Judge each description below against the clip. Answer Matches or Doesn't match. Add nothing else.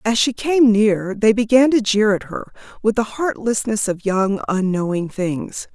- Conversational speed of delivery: Matches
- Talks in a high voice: Matches